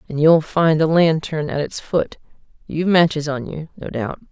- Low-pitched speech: No, medium, 155 Hz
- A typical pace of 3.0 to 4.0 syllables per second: No, 4.9 syllables/s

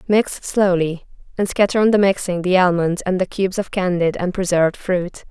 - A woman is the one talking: Yes, female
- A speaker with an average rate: Yes, average, 190 wpm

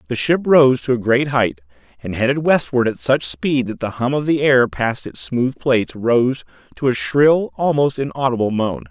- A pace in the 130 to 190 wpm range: No, average, 200 wpm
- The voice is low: Yes, low, 125 Hz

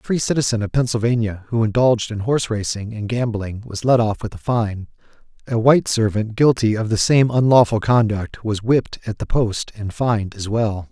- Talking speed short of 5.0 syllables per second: No, 5.4 syllables/s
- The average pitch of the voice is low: Yes, low, 110 Hz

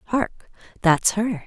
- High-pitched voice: Yes, high, 205 Hz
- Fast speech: No, slow, 125 wpm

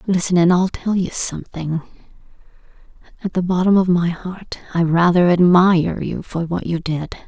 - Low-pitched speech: No, medium, 175 Hz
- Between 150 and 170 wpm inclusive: Yes, average, 155 wpm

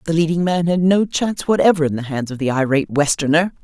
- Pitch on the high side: No, medium, 160 Hz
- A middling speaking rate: No, fast, 230 wpm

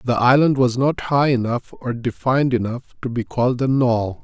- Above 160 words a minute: Yes, average, 200 wpm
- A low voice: Yes, low, 125 Hz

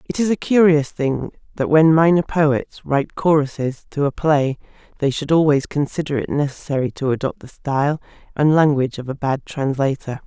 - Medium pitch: Yes, medium, 145 Hz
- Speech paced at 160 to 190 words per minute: Yes, average, 175 wpm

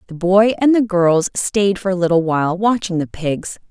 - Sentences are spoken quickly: Yes, fast, 210 wpm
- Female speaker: Yes, female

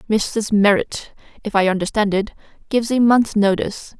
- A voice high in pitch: Yes, high, 210 Hz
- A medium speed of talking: Yes, average, 150 wpm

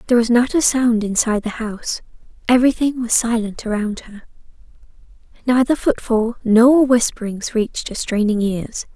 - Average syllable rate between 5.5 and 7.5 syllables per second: No, 5.1 syllables/s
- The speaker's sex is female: Yes, female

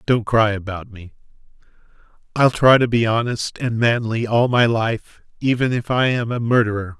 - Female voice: No, male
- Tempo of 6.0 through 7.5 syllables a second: No, 4.7 syllables/s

